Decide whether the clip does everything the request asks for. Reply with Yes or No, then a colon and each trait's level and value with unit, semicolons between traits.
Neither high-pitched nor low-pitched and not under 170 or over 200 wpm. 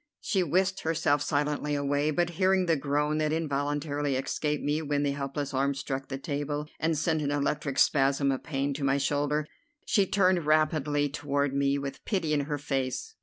Yes: medium, 145 Hz; average, 180 wpm